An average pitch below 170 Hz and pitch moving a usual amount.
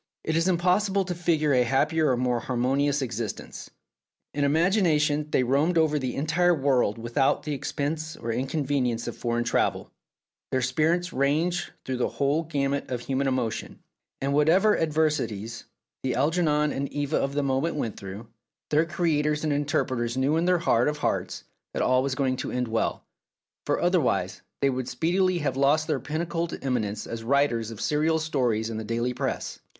Yes: medium, 140 Hz; average, 4.1 semitones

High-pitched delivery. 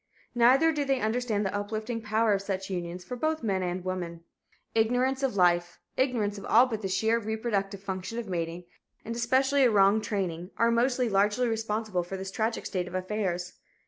Yes: high, 210 Hz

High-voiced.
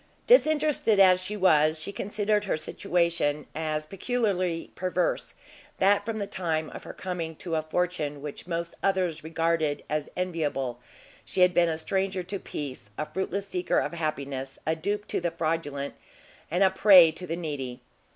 No: medium, 170 Hz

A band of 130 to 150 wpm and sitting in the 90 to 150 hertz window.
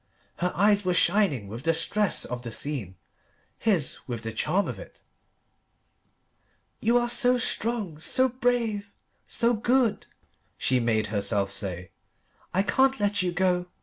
No: average, 145 wpm; medium, 185 Hz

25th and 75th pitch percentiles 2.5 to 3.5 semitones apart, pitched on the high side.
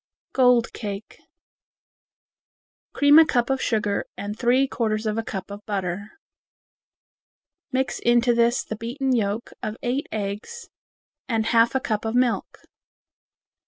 Yes: average, 2.9 semitones; high, 230 Hz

